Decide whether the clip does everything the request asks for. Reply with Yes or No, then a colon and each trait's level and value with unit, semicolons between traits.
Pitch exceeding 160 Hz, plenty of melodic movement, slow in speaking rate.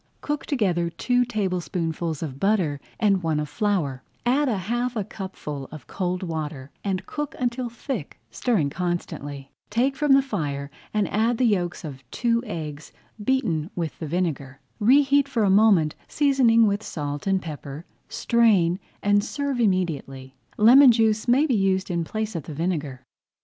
No: high, 190 Hz; wide, 7.0 semitones; average, 155 wpm